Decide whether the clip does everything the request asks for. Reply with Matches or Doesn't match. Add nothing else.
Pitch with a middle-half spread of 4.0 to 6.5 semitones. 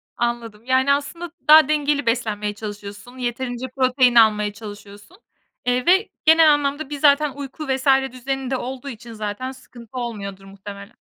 Matches